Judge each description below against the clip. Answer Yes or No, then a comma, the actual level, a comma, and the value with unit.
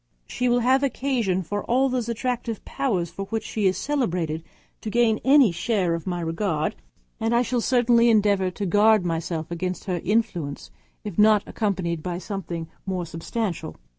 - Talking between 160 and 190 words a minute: Yes, average, 165 wpm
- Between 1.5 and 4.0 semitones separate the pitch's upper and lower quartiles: No, average, 5.1 semitones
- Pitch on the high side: Yes, high, 205 Hz